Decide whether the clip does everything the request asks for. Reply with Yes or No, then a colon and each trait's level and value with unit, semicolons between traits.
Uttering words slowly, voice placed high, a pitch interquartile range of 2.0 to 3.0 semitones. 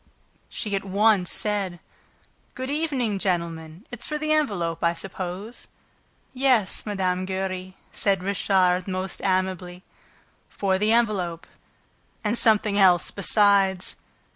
Yes: slow, 115 wpm; high, 195 Hz; average, 2.7 semitones